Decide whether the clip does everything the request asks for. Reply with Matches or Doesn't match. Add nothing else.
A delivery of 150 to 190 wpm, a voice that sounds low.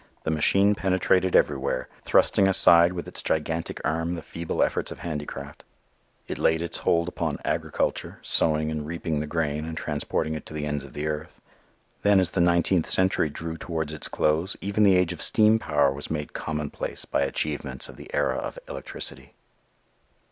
Matches